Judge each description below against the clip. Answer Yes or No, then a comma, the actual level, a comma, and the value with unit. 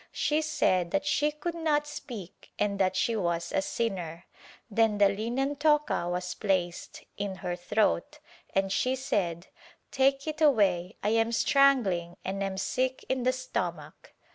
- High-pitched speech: Yes, high, 210 Hz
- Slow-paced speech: No, average, 155 wpm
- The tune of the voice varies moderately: No, wide, 6.8 semitones